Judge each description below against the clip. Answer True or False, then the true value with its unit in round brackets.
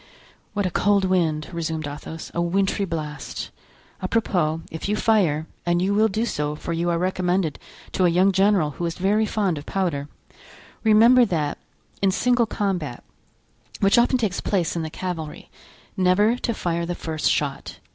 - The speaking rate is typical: True (160 wpm)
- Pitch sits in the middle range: True (180 Hz)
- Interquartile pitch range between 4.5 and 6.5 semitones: False (4.0 semitones)